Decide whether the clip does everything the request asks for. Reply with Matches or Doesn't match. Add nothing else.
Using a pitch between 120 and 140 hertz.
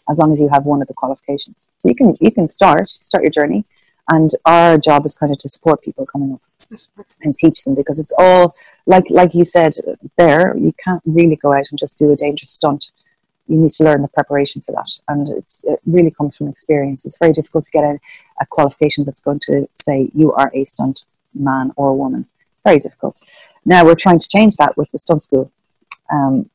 Doesn't match